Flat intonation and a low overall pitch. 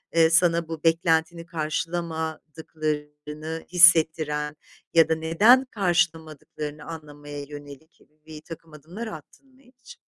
No: narrow, 1.9 semitones; medium, 160 Hz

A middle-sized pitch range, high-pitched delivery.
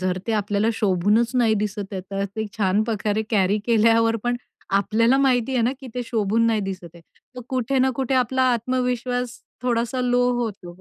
Yes: average, 3.3 semitones; high, 225 Hz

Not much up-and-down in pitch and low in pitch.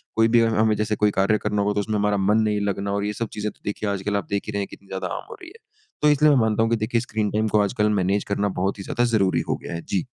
Yes: narrow, 1.6 semitones; low, 105 Hz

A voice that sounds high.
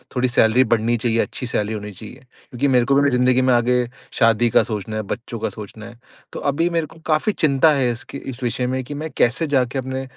No: low, 125 Hz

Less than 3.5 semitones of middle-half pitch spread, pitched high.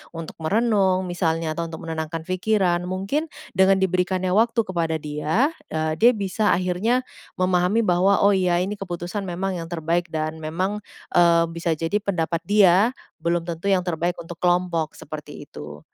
No: average, 2.8 semitones; medium, 180 Hz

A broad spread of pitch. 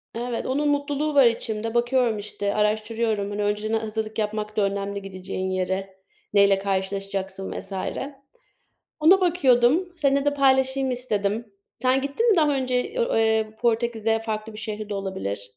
No: average, 4.5 semitones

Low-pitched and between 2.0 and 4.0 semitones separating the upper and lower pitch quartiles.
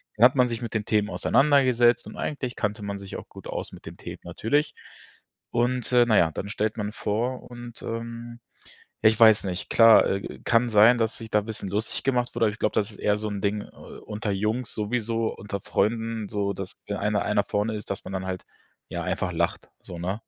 Yes: low, 110 Hz; narrow, 2.5 semitones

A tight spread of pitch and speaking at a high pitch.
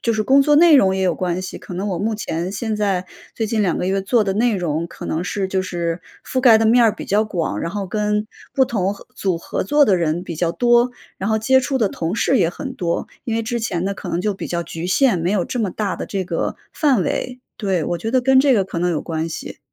No: average, 4.6 semitones; high, 200 Hz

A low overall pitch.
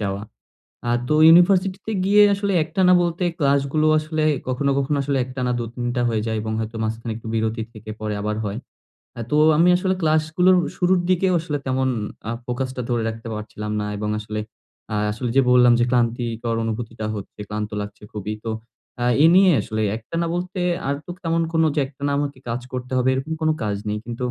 Yes: low, 125 Hz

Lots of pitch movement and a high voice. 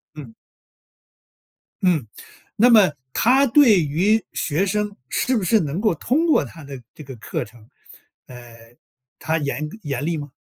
No: wide, 7.3 semitones; medium, 160 Hz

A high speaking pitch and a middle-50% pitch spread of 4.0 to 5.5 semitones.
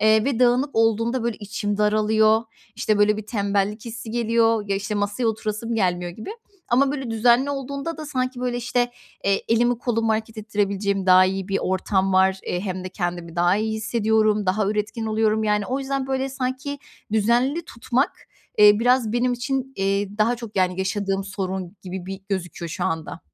No: high, 215 Hz; average, 3.5 semitones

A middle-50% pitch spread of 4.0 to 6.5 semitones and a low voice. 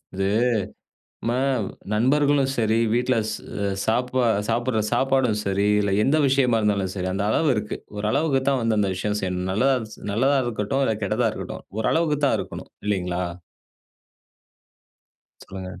Yes: average, 4.5 semitones; low, 115 Hz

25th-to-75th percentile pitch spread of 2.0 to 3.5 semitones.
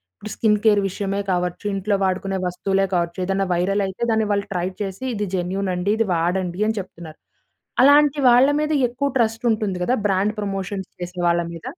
Yes: average, 3.0 semitones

